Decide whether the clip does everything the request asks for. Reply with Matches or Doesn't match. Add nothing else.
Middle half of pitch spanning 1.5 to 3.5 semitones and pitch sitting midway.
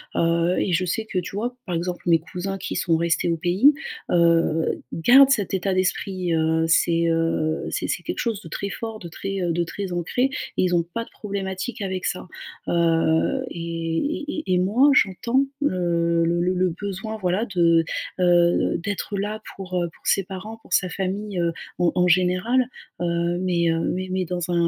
Matches